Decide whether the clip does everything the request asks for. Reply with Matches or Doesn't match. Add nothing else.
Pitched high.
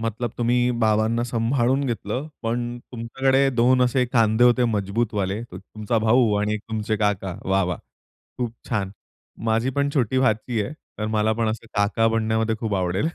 Doesn't match